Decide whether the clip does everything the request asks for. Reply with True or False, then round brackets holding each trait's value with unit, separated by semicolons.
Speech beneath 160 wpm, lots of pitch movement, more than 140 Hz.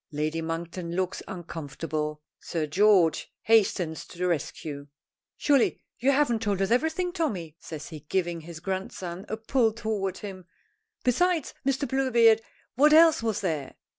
True (140 wpm; 6.3 semitones; 190 Hz)